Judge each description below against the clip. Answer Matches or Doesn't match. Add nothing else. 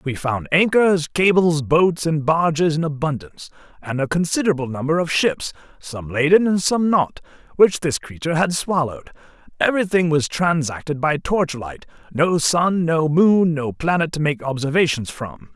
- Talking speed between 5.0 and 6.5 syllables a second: Doesn't match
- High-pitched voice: Doesn't match